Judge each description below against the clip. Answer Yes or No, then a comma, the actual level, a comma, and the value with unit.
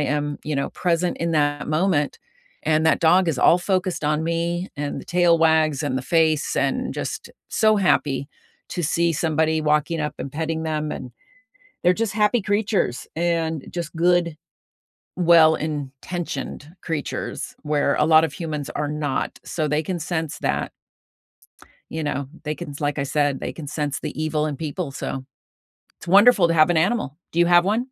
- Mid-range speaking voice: Yes, medium, 160 Hz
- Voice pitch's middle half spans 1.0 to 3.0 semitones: Yes, average, 2.7 semitones